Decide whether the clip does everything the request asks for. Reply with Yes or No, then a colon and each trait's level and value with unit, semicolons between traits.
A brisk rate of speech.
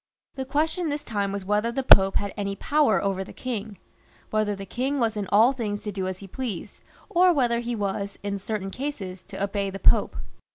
Yes: fast, 210 wpm